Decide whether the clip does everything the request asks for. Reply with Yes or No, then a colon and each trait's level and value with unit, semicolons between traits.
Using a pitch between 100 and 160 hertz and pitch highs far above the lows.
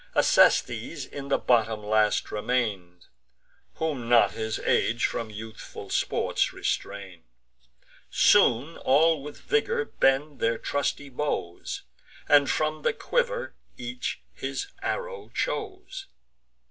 Yes: low, 135 Hz; wide, 6.5 semitones